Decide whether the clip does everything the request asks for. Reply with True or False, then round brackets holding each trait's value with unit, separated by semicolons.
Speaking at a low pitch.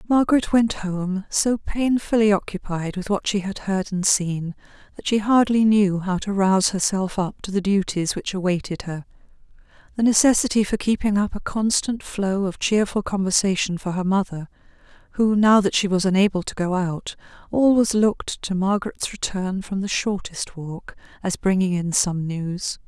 False (195 Hz)